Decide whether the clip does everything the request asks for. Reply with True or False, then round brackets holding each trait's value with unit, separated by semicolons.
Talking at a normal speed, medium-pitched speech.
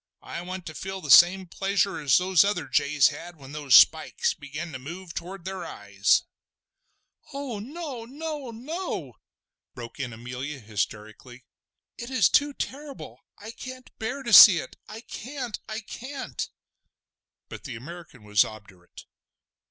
True (145 wpm; 175 Hz)